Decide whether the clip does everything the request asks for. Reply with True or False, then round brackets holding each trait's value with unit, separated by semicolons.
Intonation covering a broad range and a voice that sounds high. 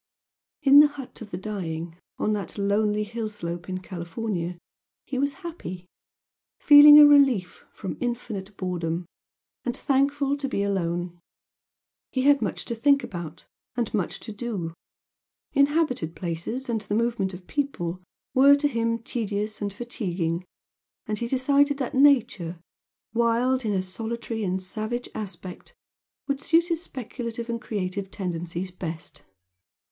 True (6.0 semitones; 215 Hz)